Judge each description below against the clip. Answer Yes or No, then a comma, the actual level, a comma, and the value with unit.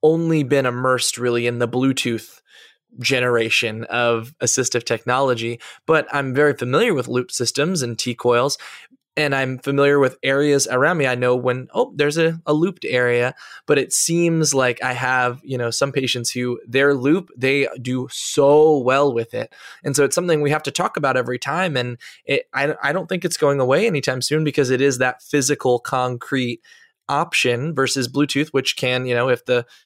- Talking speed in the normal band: Yes, average, 185 wpm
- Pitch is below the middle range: Yes, low, 130 Hz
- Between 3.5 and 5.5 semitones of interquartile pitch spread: No, average, 2.8 semitones